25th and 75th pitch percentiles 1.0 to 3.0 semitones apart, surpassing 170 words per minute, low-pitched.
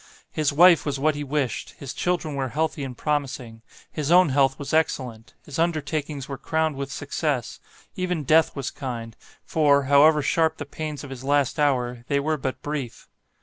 No: narrow, 2.6 semitones; average, 180 wpm; medium, 145 Hz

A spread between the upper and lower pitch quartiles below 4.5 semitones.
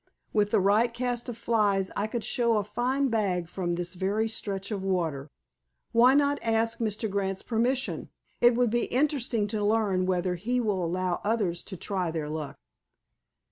Yes: average, 4.0 semitones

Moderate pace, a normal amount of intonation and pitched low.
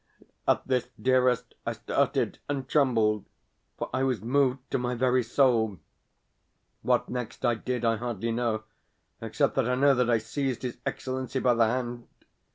No: average, 165 wpm; narrow, 2.0 semitones; low, 125 Hz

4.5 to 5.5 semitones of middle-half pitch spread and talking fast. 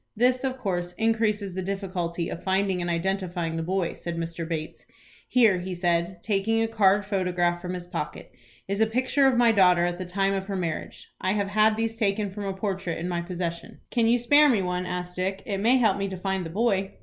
No: average, 3.4 semitones; fast, 220 wpm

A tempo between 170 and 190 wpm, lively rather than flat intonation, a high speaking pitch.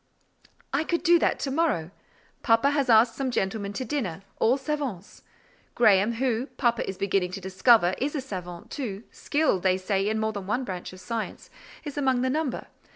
Yes: average, 175 wpm; wide, 5.8 semitones; high, 230 Hz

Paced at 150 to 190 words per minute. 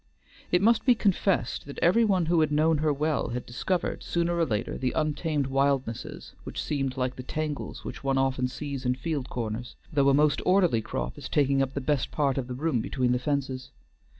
No: fast, 205 wpm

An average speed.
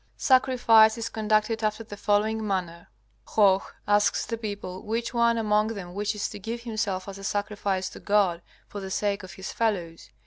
Yes: average, 175 wpm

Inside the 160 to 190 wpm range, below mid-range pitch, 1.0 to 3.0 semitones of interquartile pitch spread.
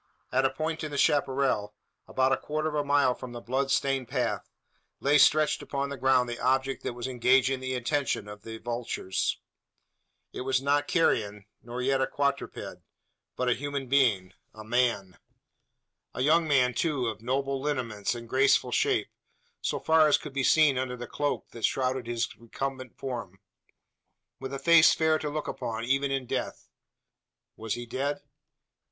Yes: average, 170 wpm; low, 130 Hz; average, 2.7 semitones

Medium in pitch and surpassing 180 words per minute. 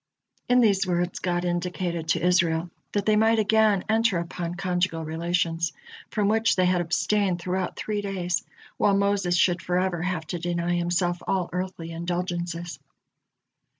No: medium, 180 Hz; average, 150 wpm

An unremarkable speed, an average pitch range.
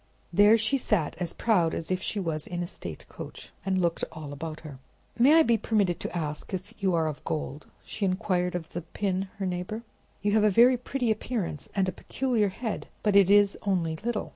No: fast, 215 wpm; average, 4.2 semitones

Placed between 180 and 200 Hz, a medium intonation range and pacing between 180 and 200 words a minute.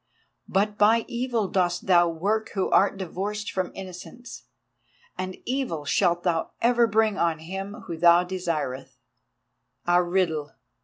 No: medium, 185 Hz; average, 3.4 semitones; slow, 135 wpm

